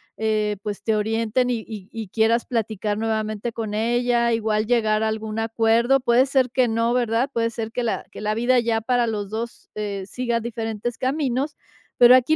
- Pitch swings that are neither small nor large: No, narrow, 1.9 semitones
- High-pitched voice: Yes, high, 225 Hz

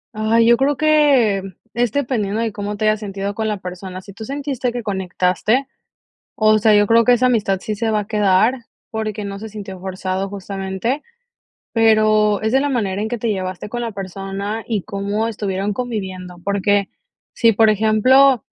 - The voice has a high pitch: Yes, high, 215 Hz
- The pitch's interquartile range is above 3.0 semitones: No, average, 2.7 semitones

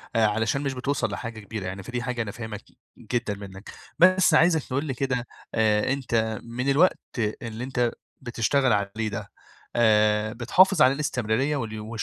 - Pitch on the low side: Yes, low, 120 Hz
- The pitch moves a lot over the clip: No, average, 3.8 semitones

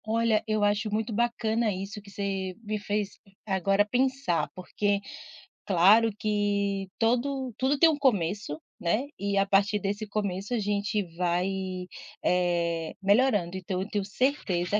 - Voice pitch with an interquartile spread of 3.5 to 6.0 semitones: No, narrow, 2.5 semitones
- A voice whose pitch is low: No, high, 205 Hz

